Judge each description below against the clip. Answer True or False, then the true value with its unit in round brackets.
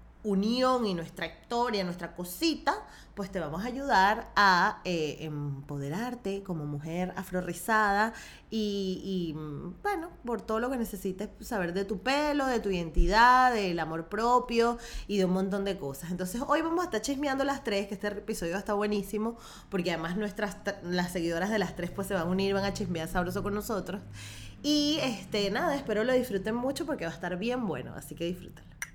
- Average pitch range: True (4.7 semitones)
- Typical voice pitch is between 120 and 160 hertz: False (200 Hz)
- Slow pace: False (185 wpm)